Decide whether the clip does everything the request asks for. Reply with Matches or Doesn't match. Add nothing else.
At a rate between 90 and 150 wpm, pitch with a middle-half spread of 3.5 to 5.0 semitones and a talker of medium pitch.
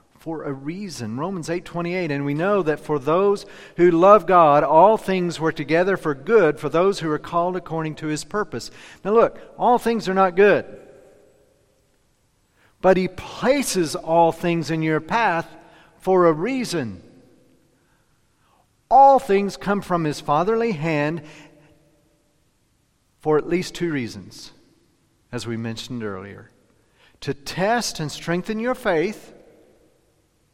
Matches